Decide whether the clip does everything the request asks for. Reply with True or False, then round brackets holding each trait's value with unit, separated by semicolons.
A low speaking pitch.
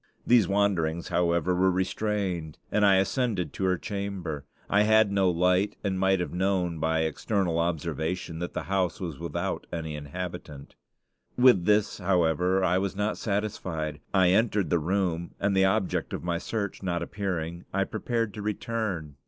True (95 Hz)